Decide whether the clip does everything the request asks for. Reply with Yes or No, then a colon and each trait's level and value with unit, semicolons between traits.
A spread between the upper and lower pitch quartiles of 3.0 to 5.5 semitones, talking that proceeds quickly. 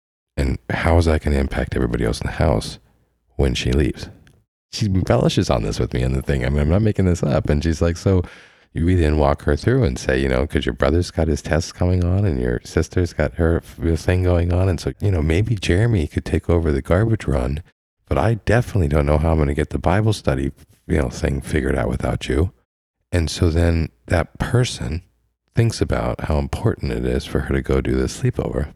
Yes: average, 4.6 semitones; fast, 230 wpm